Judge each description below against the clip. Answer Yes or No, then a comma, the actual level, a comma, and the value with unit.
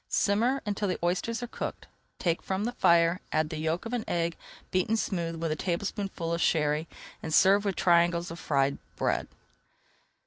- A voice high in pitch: No, medium, 175 Hz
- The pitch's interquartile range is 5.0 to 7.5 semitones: No, average, 3.4 semitones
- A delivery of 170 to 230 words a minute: Yes, average, 175 wpm